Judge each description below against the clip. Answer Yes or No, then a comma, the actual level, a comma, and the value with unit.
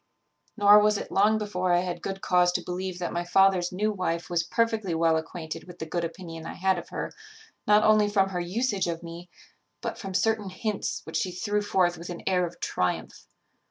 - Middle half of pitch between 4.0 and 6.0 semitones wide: No, average, 3.0 semitones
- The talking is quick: Yes, fast, 210 wpm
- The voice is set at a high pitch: No, medium, 180 Hz